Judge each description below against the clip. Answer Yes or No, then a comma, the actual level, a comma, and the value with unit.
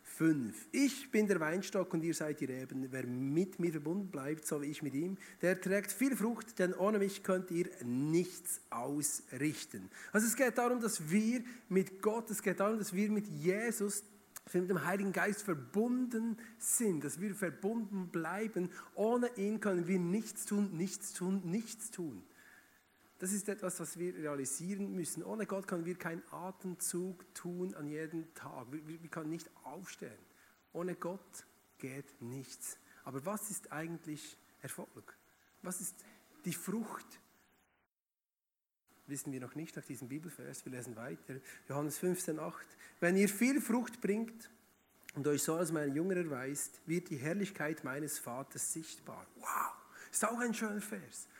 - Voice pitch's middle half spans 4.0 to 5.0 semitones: Yes, average, 4.7 semitones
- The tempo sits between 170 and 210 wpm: No, average, 160 wpm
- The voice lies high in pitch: No, medium, 180 Hz